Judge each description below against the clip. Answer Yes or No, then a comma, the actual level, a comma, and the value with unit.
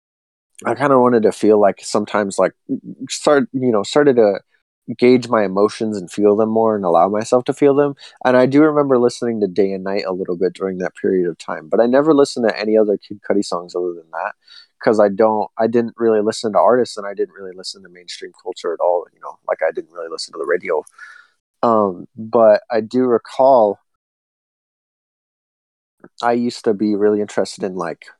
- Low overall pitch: Yes, low, 115 Hz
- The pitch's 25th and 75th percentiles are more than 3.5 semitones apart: Yes, average, 5.2 semitones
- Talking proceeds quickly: Yes, fast, 210 wpm